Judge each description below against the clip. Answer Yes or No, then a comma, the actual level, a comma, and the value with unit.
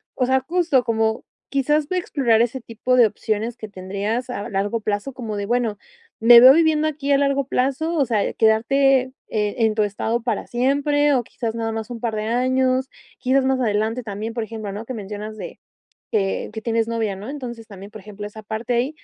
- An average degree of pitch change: Yes, average, 3.3 semitones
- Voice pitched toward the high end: Yes, high, 230 Hz